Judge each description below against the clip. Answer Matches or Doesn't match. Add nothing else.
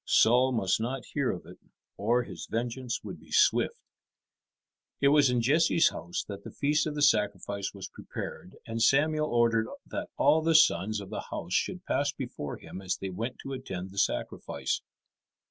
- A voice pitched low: Matches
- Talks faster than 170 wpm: Matches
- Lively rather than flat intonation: Matches